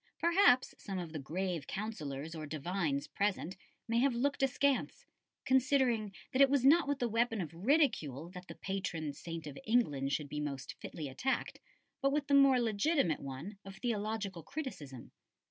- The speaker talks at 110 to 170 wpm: Yes, average, 165 wpm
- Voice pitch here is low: No, high, 200 Hz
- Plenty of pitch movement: Yes, wide, 8.9 semitones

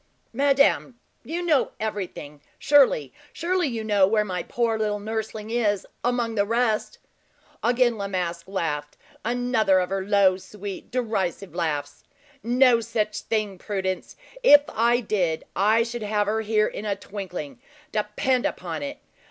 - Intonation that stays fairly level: No, average, 3.9 semitones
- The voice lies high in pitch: Yes, high, 215 Hz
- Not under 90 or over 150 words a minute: Yes, average, 145 wpm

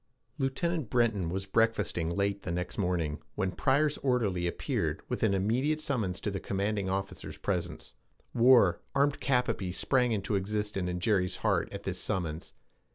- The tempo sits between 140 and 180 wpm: Yes, average, 160 wpm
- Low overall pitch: Yes, low, 100 Hz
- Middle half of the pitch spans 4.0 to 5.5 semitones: Yes, average, 5.2 semitones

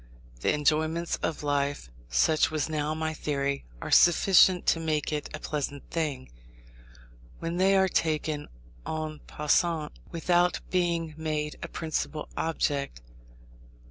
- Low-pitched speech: No, medium, 155 Hz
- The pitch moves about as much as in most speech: No, narrow, 2.0 semitones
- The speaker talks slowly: Yes, slow, 125 wpm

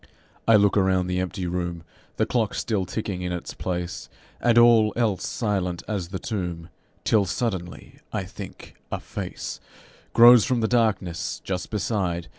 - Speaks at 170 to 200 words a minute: No, average, 155 wpm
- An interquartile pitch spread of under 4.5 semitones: Yes, average, 3.7 semitones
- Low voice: Yes, very low, 95 Hz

